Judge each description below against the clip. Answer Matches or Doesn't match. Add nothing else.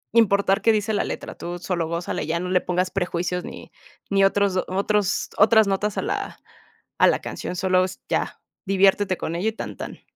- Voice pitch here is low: Doesn't match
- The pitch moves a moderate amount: Doesn't match